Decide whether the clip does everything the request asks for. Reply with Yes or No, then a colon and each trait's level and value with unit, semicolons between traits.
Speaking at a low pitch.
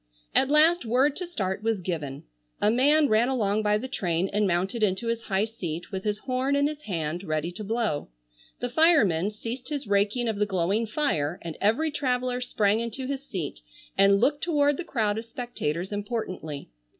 No: high, 220 Hz